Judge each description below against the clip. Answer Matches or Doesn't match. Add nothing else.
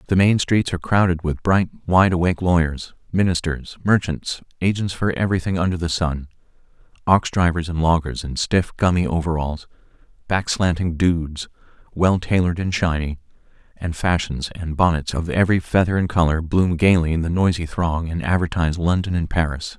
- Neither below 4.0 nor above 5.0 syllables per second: Doesn't match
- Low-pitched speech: Matches